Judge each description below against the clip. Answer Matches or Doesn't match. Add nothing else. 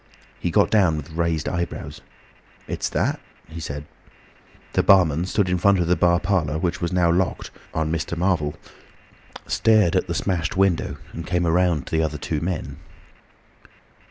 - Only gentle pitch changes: Matches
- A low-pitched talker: Matches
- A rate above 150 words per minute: Matches